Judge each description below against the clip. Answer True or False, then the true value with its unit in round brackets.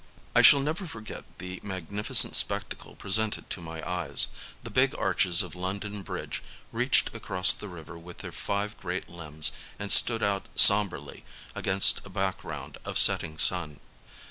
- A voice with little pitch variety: False (3.3 semitones)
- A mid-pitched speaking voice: False (95 Hz)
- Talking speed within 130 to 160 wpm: True (150 wpm)